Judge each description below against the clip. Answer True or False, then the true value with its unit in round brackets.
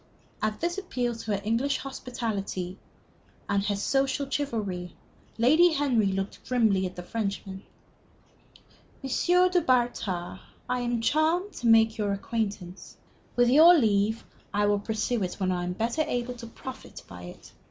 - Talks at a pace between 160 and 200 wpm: False (150 wpm)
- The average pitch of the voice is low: False (225 Hz)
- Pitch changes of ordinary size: True (4.5 semitones)